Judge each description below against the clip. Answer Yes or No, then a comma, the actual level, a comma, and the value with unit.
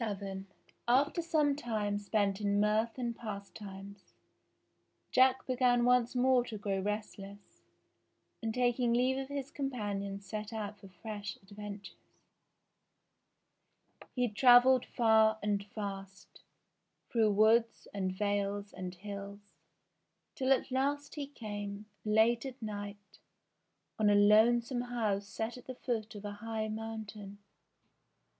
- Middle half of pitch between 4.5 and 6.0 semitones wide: No, average, 3.2 semitones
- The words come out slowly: Yes, slow, 125 wpm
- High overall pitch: Yes, high, 215 Hz